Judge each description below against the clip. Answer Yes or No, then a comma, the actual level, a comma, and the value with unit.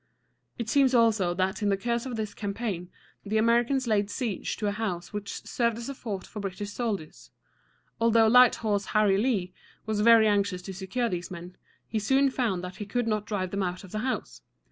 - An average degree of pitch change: Yes, average, 3.3 semitones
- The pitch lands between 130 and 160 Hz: No, high, 210 Hz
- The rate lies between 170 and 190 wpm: No, fast, 205 wpm